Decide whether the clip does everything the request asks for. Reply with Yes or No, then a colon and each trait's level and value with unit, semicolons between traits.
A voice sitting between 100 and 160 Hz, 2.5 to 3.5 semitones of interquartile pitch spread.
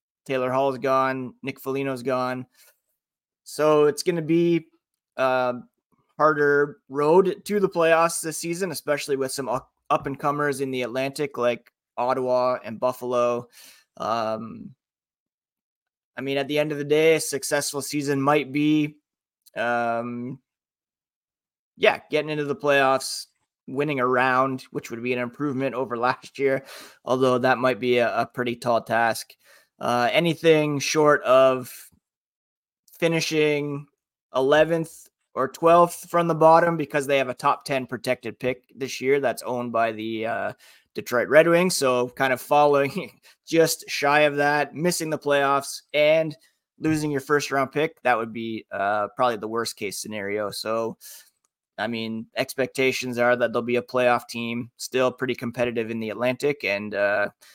Yes: low, 135 Hz; average, 3.2 semitones